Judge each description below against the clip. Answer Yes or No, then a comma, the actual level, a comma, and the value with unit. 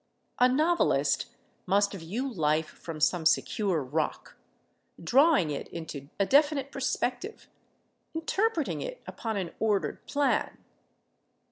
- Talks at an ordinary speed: No, slow, 110 wpm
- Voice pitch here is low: No, high, 215 Hz